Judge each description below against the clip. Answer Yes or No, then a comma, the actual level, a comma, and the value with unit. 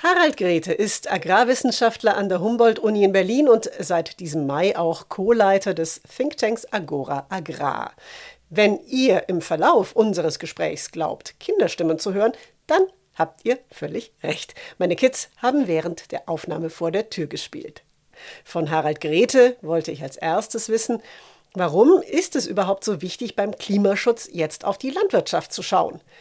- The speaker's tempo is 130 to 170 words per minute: Yes, average, 150 wpm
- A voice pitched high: Yes, high, 200 Hz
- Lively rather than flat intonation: Yes, wide, 6.7 semitones